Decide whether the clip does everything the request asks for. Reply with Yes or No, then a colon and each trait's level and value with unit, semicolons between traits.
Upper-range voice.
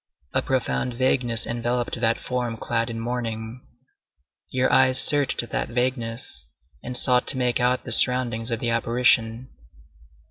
No: low, 120 Hz